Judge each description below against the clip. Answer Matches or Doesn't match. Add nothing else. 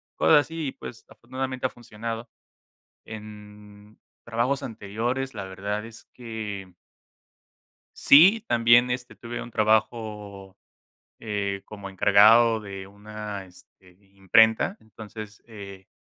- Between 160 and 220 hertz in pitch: Doesn't match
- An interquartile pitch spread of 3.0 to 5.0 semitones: Doesn't match